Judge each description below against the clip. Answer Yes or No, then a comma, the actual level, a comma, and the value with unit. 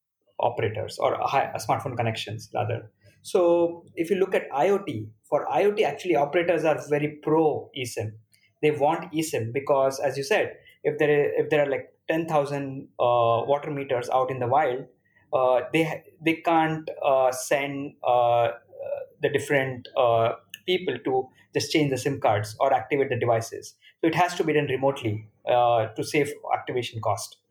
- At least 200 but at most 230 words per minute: No, average, 170 wpm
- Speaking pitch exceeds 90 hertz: Yes, medium, 140 Hz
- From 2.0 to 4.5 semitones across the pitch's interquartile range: No, average, 5.2 semitones